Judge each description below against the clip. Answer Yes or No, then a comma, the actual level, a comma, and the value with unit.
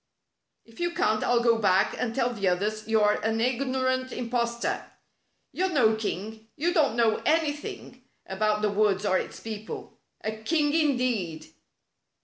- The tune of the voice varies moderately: Yes, average, 3.4 semitones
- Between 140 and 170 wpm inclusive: Yes, average, 160 wpm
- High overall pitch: Yes, high, 230 Hz